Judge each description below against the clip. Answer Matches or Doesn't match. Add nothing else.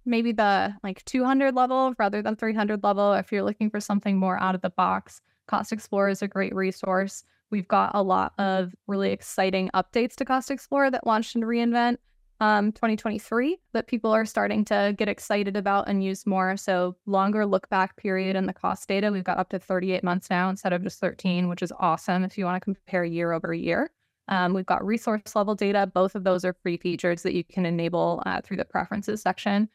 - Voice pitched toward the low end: Doesn't match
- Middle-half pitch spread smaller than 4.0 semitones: Matches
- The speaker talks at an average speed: Doesn't match